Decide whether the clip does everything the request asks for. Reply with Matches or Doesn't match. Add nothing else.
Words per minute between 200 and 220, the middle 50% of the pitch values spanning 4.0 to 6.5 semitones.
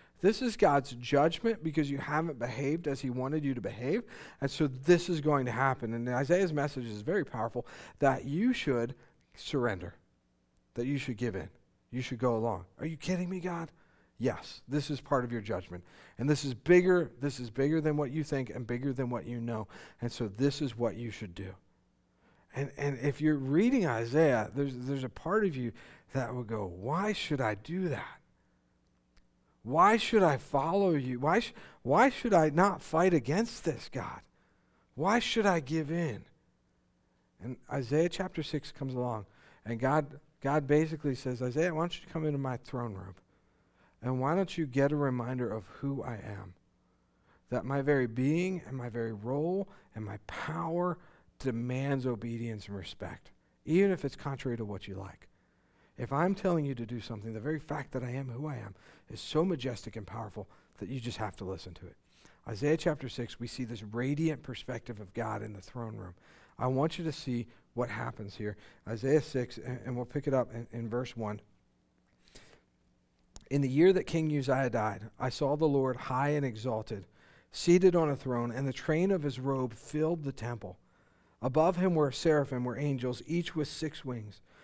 Doesn't match